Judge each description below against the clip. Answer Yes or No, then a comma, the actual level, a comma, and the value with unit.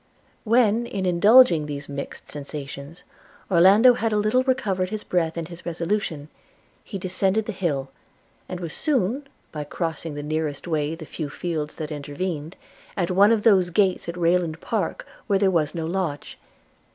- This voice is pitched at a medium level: Yes, medium, 175 Hz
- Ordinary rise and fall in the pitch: Yes, average, 4.7 semitones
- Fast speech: No, average, 165 wpm